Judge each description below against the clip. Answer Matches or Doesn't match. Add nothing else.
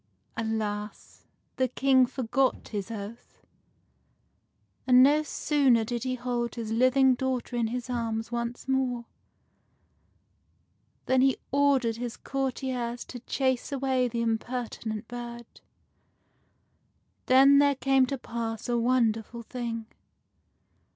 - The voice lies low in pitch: Doesn't match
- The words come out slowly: Matches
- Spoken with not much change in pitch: Matches